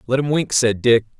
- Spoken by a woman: No, male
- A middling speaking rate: No, fast, 250 wpm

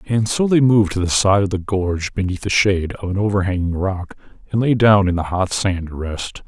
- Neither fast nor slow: No, fast, 240 wpm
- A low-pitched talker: Yes, low, 100 Hz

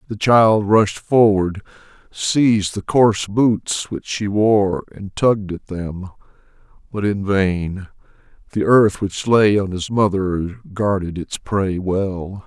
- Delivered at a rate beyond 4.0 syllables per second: No, 3.5 syllables/s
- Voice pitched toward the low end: Yes, low, 100 Hz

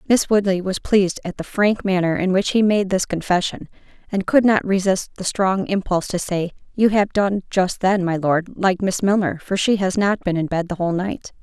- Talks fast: Yes, fast, 225 wpm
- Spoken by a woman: Yes, female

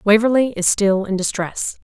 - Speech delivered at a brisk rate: No, average, 160 wpm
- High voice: Yes, high, 210 Hz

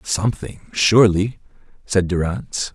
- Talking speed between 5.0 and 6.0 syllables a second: No, 4.8 syllables/s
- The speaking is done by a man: Yes, male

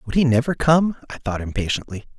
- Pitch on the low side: Yes, low, 130 Hz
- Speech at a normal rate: Yes, average, 190 wpm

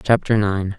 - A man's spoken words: Yes, male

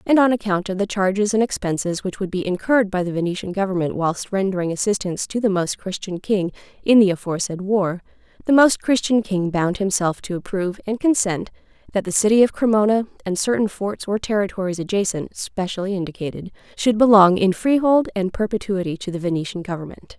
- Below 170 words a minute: No, average, 180 wpm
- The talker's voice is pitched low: No, high, 195 Hz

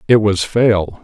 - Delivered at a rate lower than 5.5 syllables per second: Yes, 4.6 syllables/s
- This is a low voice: Yes, low, 105 Hz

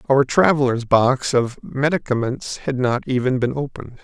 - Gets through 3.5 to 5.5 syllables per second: Yes, 4.8 syllables/s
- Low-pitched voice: Yes, low, 130 Hz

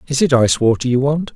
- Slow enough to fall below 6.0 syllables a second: No, 6.7 syllables/s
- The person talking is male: Yes, male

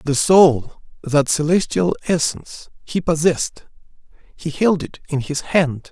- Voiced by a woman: No, male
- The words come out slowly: Yes, slow, 130 wpm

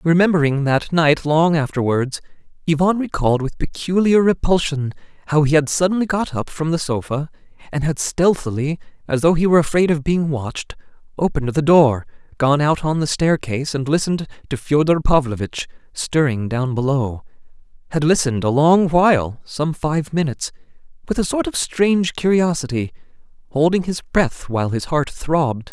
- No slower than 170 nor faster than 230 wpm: No, average, 150 wpm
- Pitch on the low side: No, medium, 155 Hz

